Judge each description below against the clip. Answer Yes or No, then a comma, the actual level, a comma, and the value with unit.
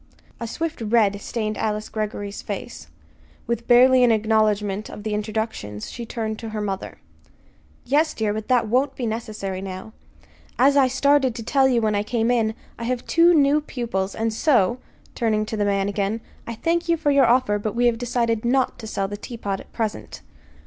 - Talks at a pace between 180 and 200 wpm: Yes, average, 190 wpm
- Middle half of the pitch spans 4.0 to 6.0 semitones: No, average, 3.0 semitones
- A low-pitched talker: No, high, 225 Hz